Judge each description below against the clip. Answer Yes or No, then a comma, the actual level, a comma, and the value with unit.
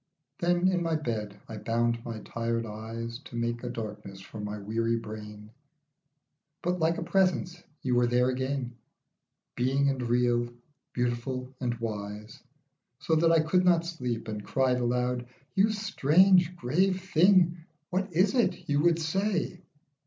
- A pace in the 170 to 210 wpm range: No, average, 150 wpm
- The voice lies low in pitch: Yes, low, 125 Hz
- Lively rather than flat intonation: Yes, wide, 6.7 semitones